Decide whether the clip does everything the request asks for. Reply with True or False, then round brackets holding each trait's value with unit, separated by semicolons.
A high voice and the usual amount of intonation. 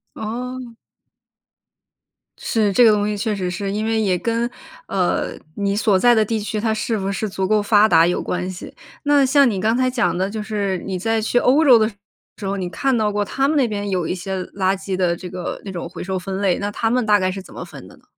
True (205 Hz; 3.0 semitones)